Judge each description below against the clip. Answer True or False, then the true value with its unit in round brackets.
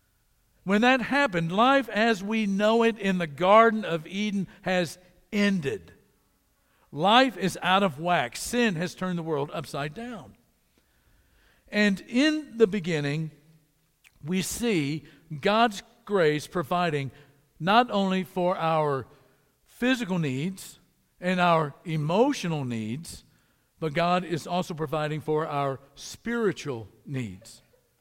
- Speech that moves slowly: True (120 wpm)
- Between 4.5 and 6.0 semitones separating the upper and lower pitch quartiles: True (5.4 semitones)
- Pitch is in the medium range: True (175 Hz)